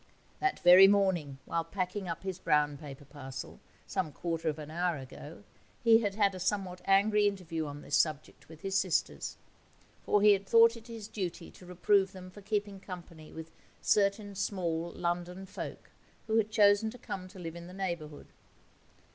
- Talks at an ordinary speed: Yes, average, 180 wpm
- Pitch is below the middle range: No, medium, 185 Hz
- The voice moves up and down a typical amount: Yes, average, 3.7 semitones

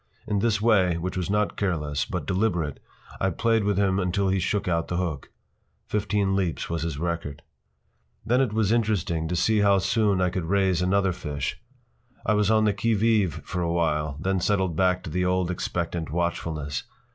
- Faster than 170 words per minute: Yes, average, 190 wpm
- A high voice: No, very low, 95 Hz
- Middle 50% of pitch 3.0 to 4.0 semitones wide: Yes, average, 3.4 semitones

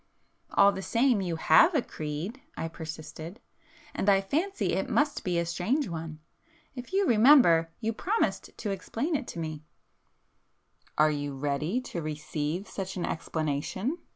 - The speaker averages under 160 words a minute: Yes, average, 145 wpm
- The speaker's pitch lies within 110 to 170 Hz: No, medium, 185 Hz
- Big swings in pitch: Yes, wide, 7.9 semitones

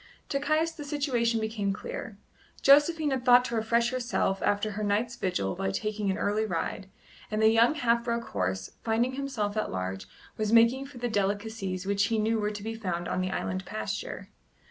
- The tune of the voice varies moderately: Yes, average, 3.5 semitones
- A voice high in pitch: Yes, high, 220 Hz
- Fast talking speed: No, average, 190 wpm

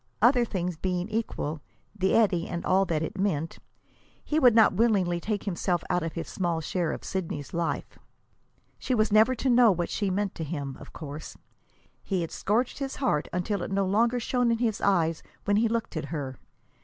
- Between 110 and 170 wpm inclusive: No, average, 195 wpm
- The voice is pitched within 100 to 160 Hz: No, high, 190 Hz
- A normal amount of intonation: Yes, average, 5.0 semitones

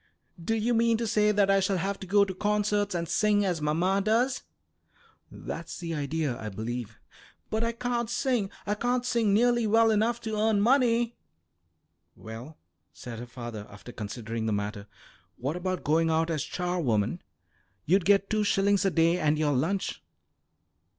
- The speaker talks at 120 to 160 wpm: No, average, 170 wpm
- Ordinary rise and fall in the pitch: No, wide, 6.5 semitones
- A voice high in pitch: Yes, high, 195 Hz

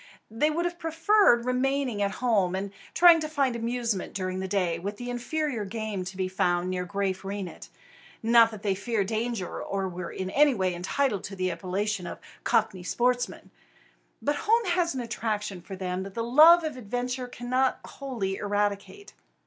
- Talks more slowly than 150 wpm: No, average, 175 wpm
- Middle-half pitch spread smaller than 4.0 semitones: No, average, 5.1 semitones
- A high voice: Yes, high, 220 Hz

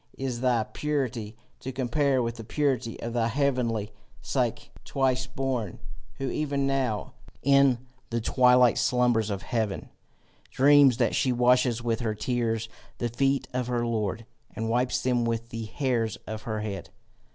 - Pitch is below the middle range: Yes, low, 120 Hz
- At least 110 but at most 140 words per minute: No, average, 150 wpm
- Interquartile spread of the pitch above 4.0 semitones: No, narrow, 2.6 semitones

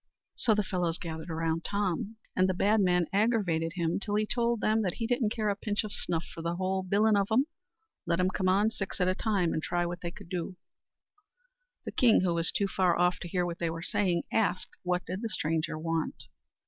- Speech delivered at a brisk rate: Yes, fast, 225 wpm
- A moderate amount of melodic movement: Yes, average, 3.6 semitones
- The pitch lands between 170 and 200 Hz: Yes, medium, 185 Hz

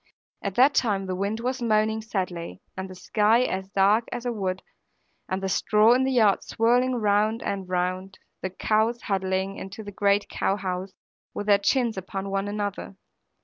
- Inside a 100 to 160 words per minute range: No, average, 180 wpm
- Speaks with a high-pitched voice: Yes, high, 200 Hz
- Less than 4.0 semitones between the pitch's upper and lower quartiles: Yes, narrow, 2.6 semitones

